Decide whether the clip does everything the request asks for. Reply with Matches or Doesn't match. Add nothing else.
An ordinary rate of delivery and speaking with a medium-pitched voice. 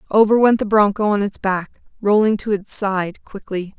Doesn't match